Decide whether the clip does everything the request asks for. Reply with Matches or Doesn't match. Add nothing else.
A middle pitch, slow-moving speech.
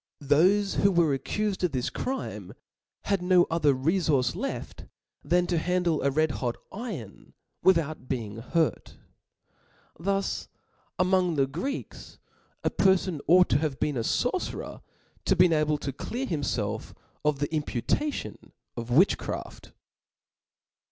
Matches